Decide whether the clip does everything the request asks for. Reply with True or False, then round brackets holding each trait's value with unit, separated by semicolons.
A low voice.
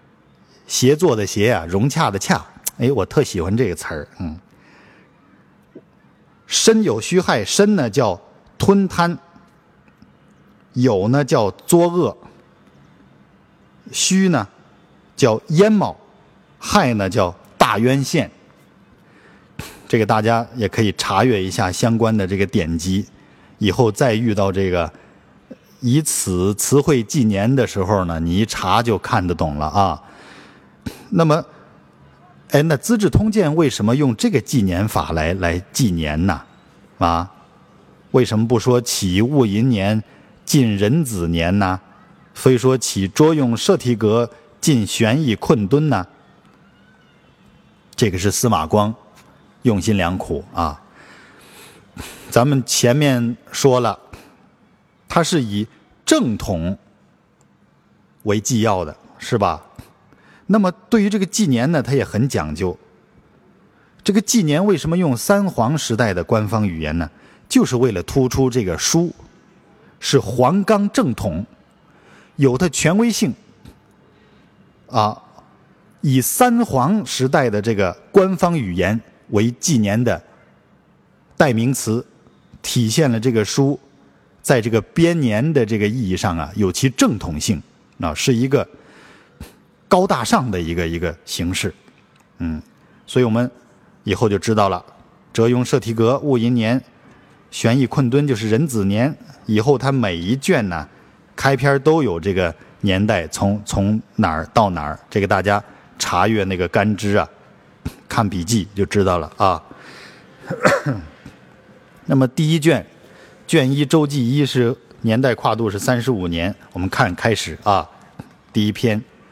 True (115 Hz)